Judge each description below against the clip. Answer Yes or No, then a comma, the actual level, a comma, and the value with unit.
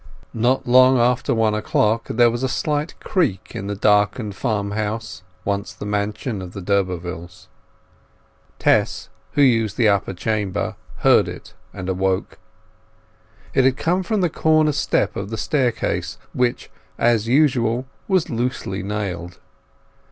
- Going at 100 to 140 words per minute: Yes, slow, 135 wpm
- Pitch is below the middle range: Yes, low, 110 Hz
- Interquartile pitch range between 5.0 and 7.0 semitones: No, average, 4.2 semitones